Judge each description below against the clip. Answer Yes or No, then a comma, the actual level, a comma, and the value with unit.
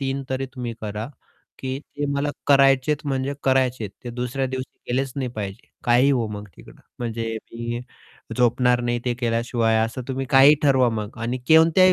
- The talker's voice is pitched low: Yes, low, 125 Hz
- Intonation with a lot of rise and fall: No, narrow, 2.4 semitones